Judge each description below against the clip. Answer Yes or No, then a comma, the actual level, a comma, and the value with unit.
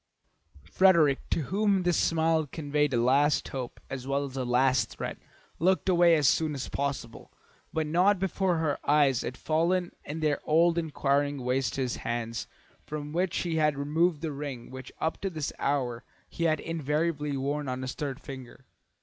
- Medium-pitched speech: Yes, medium, 150 Hz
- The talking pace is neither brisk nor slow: Yes, average, 175 wpm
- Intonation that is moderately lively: Yes, average, 3.6 semitones